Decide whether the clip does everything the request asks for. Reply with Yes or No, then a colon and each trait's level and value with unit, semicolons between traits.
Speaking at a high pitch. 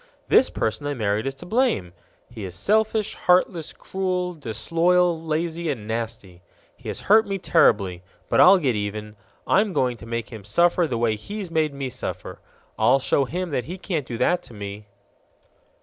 No: medium, 140 Hz